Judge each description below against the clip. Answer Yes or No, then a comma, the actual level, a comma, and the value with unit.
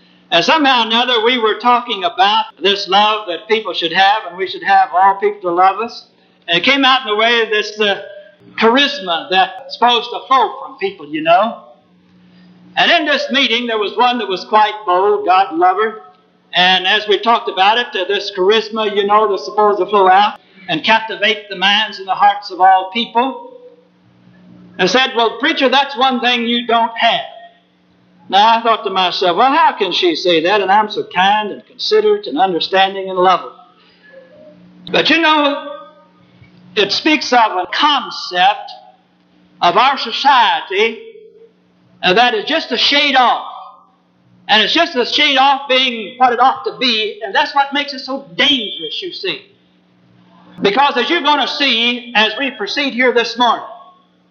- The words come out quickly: No, average, 180 wpm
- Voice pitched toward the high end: Yes, high, 230 Hz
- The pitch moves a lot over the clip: Yes, wide, 7.3 semitones